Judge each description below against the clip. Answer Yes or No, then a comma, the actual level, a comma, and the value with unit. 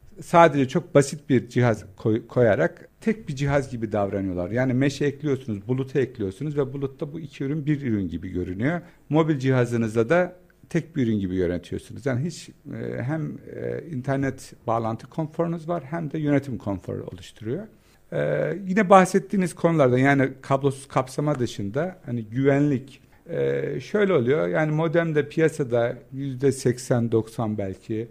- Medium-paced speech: Yes, average, 130 wpm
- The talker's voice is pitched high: No, low, 135 Hz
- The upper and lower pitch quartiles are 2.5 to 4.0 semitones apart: No, average, 5.3 semitones